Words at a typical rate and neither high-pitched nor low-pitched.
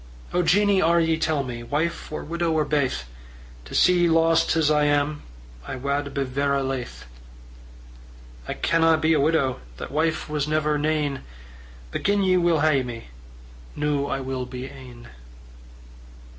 Yes: average, 160 wpm; medium, 150 Hz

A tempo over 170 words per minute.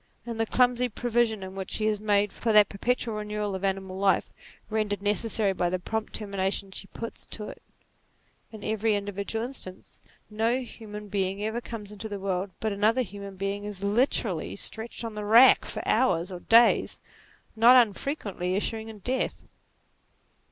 No: average, 165 wpm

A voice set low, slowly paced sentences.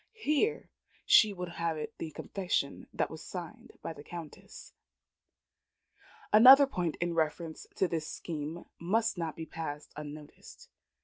No: medium, 170 Hz; slow, 130 wpm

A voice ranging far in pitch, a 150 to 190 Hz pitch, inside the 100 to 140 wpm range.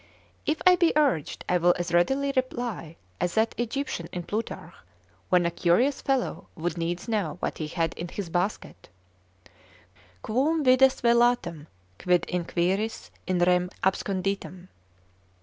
Yes: wide, 5.9 semitones; medium, 185 Hz; slow, 135 wpm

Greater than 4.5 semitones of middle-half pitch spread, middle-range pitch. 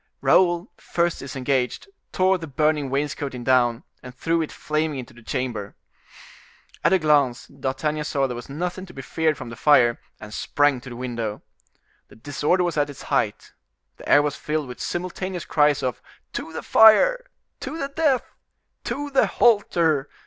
Yes: average, 5.2 semitones; medium, 150 Hz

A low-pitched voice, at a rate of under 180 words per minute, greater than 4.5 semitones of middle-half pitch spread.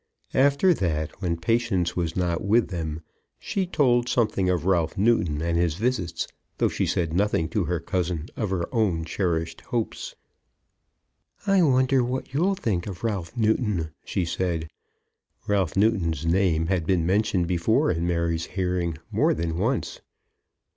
Yes: very low, 90 Hz; average, 150 wpm; average, 5.2 semitones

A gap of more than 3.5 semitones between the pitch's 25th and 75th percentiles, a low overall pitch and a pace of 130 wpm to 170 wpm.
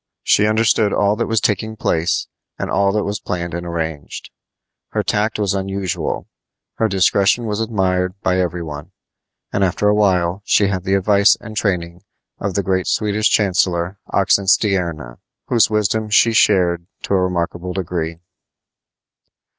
No: average, 3.0 semitones; very low, 95 Hz; average, 150 wpm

